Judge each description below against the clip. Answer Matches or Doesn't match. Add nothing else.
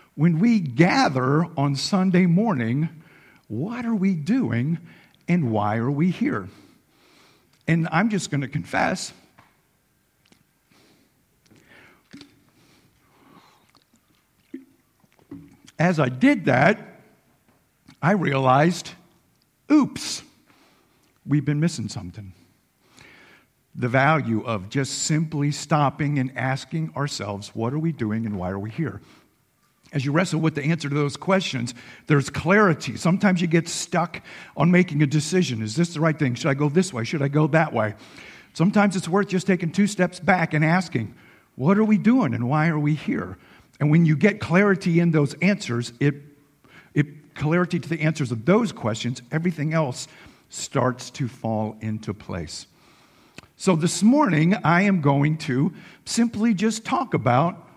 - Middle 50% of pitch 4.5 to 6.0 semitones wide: Matches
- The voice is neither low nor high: Matches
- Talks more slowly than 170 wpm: Matches